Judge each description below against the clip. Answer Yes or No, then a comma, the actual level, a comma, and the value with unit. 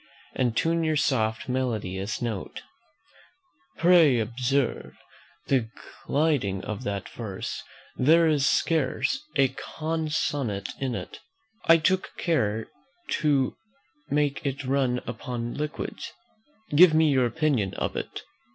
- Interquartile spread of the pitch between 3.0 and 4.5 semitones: No, average, 5.0 semitones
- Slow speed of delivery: Yes, slow, 115 wpm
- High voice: No, low, 135 Hz